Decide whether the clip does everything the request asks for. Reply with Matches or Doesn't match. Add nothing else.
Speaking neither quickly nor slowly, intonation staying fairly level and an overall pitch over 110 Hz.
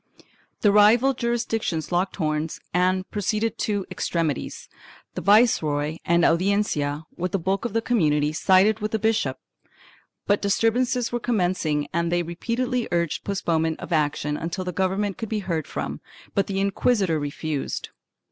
Doesn't match